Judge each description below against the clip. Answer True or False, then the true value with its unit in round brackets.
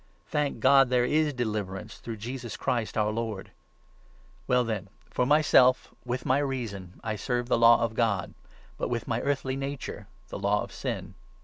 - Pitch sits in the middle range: False (120 Hz)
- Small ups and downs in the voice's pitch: False (3.2 semitones)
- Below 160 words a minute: False (175 wpm)